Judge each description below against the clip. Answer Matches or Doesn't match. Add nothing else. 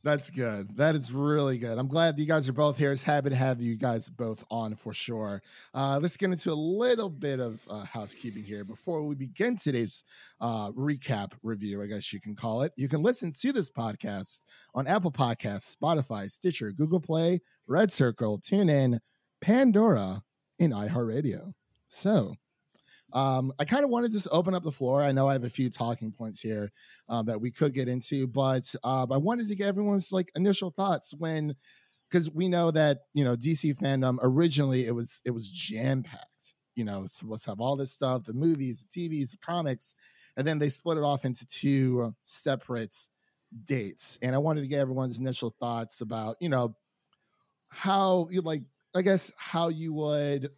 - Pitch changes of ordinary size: Doesn't match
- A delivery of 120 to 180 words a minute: Doesn't match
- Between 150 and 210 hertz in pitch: Doesn't match